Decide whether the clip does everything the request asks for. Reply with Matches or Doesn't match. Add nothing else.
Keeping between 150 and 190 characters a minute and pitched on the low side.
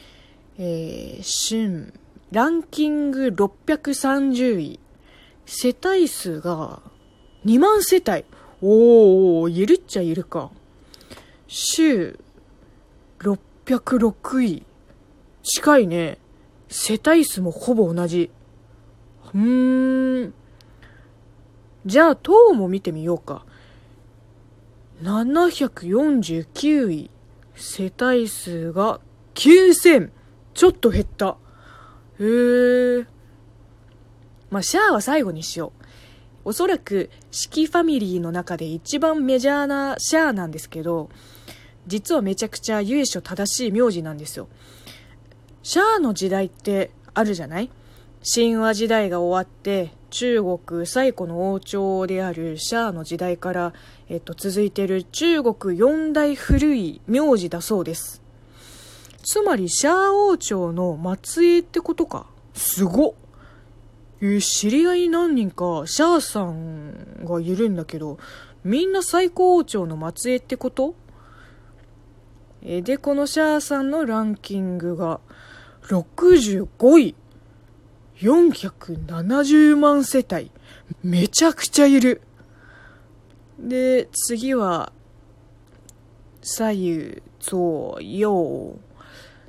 Doesn't match